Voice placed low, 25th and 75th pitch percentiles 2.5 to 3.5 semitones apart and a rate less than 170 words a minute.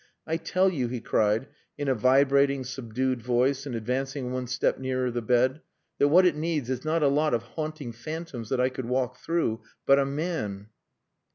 No: low, 130 Hz; average, 3.1 semitones; average, 190 wpm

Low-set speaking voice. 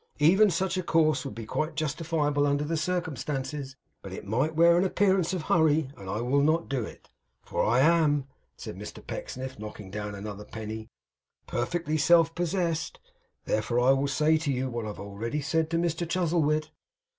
No: medium, 150 Hz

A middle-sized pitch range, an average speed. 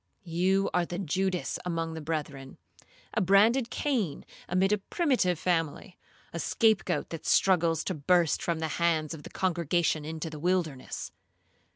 Yes: average, 3.0 semitones; average, 155 wpm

